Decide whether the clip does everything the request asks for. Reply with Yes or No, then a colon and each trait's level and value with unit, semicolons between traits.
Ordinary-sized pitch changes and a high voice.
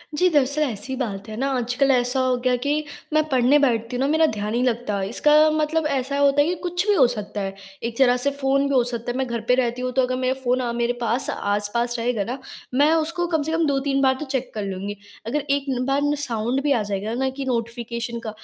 Yes: average, 3.2 semitones; very high, 255 Hz